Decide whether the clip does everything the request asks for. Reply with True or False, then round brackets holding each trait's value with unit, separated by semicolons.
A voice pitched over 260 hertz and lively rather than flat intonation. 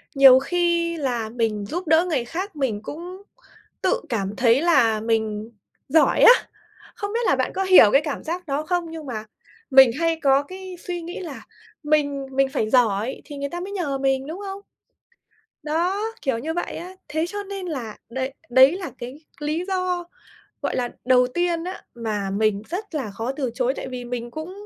True (285 Hz; 6.2 semitones)